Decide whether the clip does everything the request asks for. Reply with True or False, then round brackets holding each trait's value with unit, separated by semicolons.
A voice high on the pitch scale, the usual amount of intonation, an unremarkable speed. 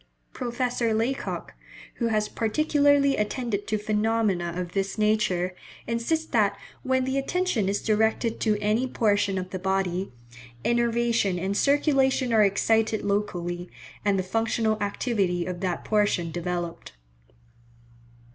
False (215 Hz; 3.7 semitones; 125 wpm)